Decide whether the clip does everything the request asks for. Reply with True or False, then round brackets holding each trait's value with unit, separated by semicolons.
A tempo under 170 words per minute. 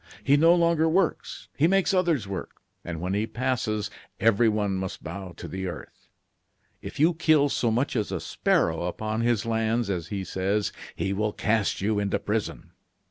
False (175 wpm)